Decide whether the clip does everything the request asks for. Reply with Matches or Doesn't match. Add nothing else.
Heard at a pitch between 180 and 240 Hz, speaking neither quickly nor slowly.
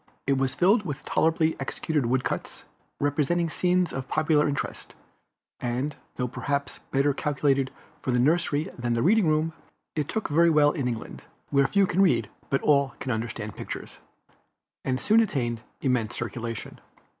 Doesn't match